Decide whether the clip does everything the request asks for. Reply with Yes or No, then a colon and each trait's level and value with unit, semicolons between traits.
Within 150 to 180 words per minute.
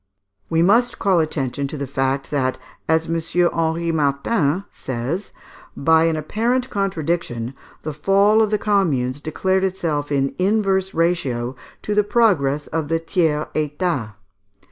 No: average, 140 wpm